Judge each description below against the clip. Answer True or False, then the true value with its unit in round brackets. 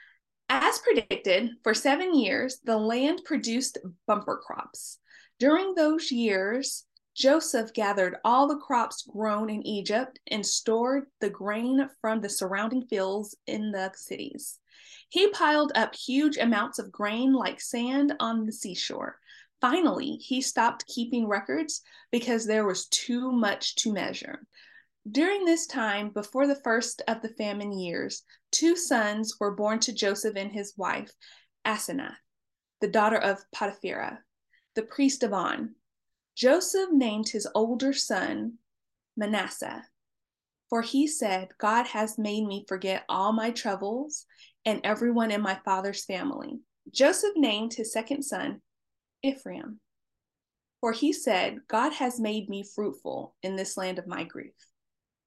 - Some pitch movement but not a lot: True (4.8 semitones)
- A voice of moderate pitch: False (230 Hz)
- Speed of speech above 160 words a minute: False (140 wpm)